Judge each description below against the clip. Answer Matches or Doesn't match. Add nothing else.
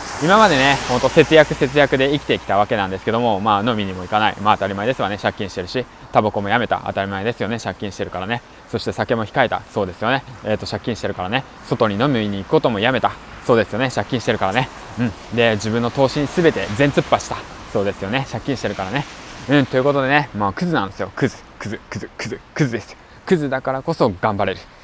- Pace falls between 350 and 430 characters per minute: Doesn't match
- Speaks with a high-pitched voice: Doesn't match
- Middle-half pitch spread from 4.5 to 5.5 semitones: Matches